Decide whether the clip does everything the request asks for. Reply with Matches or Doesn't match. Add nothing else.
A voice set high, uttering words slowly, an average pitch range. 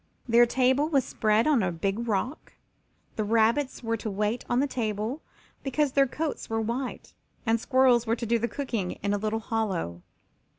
Doesn't match